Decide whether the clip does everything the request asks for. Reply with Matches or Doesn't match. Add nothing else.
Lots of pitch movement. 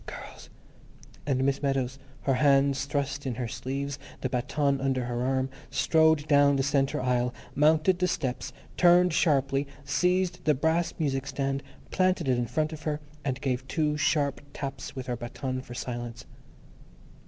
Doesn't match